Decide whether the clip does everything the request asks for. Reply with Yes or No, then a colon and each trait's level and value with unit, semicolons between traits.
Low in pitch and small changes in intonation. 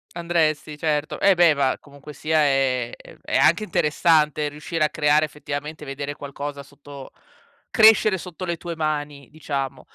No: medium, 150 Hz; narrow, 2.3 semitones